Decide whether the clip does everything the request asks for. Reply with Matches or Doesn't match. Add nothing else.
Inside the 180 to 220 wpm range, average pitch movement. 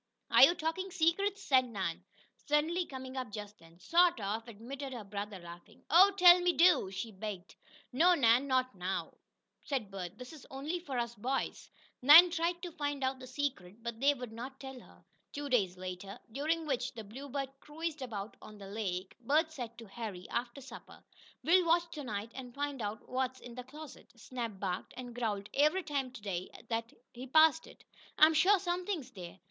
Doesn't match